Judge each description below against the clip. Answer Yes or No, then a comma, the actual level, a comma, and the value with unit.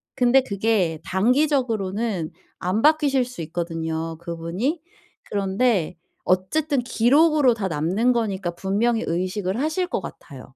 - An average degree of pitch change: No, wide, 6.1 semitones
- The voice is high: Yes, high, 205 Hz